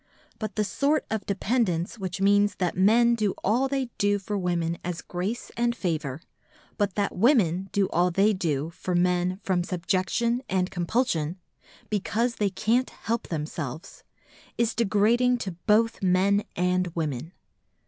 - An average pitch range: Yes, average, 4.0 semitones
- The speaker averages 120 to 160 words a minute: Yes, average, 140 wpm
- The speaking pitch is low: No, high, 195 Hz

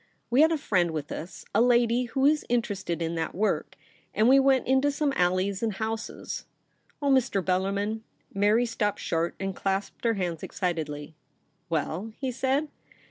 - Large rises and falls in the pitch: Yes, wide, 5.7 semitones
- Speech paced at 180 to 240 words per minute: No, average, 170 wpm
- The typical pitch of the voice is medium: No, high, 210 Hz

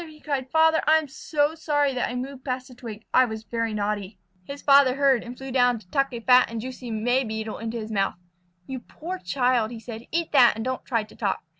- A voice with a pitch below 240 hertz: No, very high, 250 Hz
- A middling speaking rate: No, fast, 240 wpm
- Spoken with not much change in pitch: No, average, 3.7 semitones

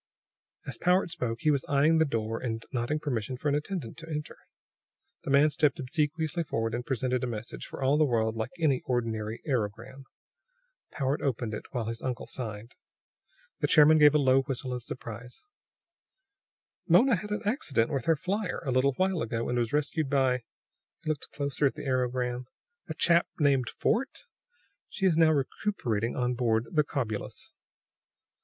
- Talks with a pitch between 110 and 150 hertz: Yes, low, 135 Hz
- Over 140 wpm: Yes, average, 175 wpm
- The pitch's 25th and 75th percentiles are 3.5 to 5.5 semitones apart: Yes, average, 4.3 semitones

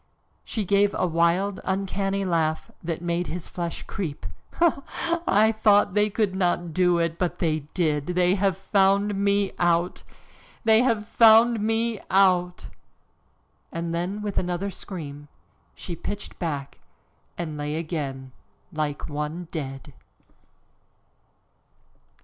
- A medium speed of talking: No, slow, 125 wpm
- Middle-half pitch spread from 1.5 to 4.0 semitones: Yes, average, 3.4 semitones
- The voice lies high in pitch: No, medium, 180 Hz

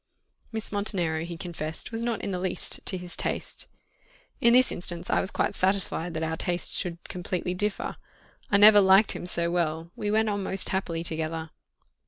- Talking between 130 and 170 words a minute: No, average, 185 wpm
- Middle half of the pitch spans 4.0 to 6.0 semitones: No, average, 3.3 semitones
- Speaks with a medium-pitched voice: Yes, medium, 180 Hz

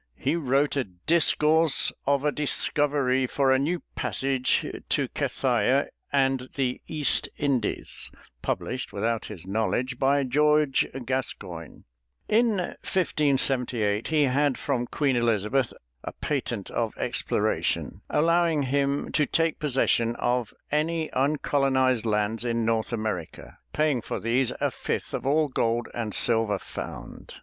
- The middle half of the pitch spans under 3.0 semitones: No, average, 3.9 semitones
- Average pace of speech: No, slow, 125 wpm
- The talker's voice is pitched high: No, low, 135 Hz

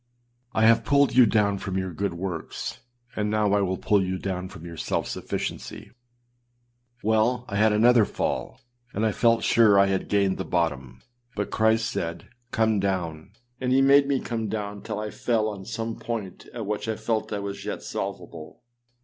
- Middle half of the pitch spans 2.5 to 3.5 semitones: Yes, average, 2.8 semitones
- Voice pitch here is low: Yes, low, 105 Hz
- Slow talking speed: No, average, 185 wpm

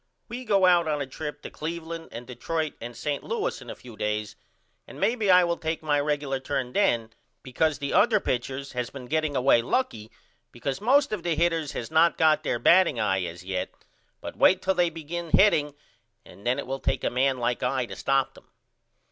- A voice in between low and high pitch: Yes, medium, 145 Hz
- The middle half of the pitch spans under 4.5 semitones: No, average, 5.3 semitones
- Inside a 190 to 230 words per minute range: Yes, fast, 205 wpm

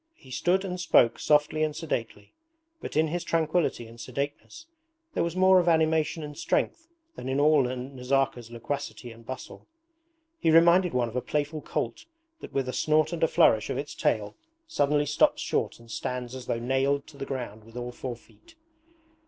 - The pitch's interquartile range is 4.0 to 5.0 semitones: Yes, average, 4.5 semitones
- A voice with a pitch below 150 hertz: Yes, medium, 140 Hz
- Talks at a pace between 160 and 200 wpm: Yes, average, 185 wpm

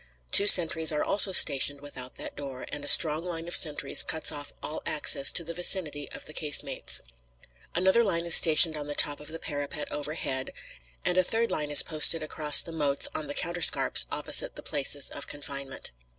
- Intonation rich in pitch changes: No, narrow, 2.6 semitones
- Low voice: No, medium, 150 Hz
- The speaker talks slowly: No, average, 195 wpm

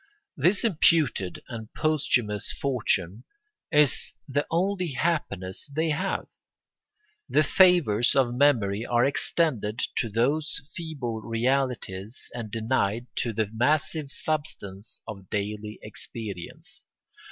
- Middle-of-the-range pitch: No, low, 120 Hz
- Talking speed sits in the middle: No, slow, 105 wpm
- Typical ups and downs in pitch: No, wide, 6.1 semitones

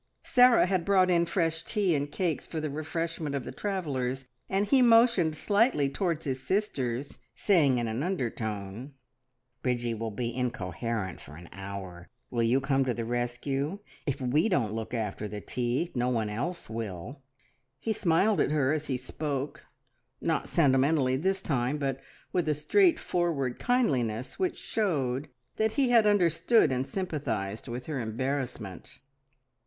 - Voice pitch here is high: No, medium, 140 Hz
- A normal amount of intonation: No, wide, 6.2 semitones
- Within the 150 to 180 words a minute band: Yes, average, 155 wpm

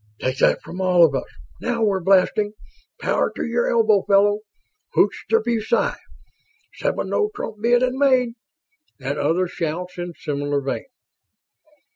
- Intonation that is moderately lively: No, wide, 5.8 semitones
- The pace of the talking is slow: No, average, 145 wpm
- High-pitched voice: Yes, high, 195 Hz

